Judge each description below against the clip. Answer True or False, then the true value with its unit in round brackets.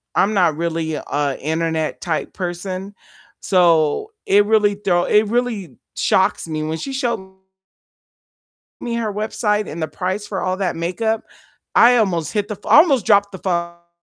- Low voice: False (190 Hz)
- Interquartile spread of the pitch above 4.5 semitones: False (3.9 semitones)